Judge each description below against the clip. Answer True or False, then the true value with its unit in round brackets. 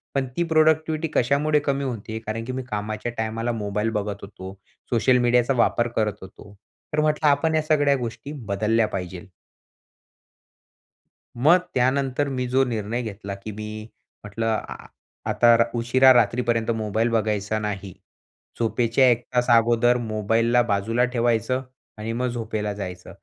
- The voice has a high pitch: False (115 Hz)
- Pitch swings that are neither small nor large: True (3.1 semitones)